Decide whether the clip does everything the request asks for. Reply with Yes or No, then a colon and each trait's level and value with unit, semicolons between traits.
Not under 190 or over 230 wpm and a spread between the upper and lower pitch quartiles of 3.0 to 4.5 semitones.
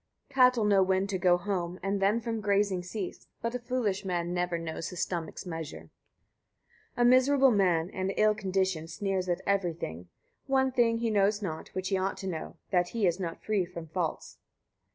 Yes: average, 195 wpm; average, 3.4 semitones